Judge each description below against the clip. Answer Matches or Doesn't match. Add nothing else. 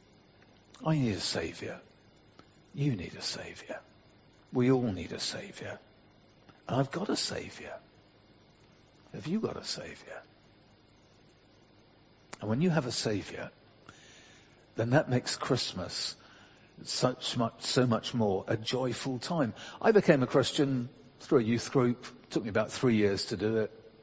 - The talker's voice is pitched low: Matches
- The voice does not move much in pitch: Doesn't match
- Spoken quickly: Doesn't match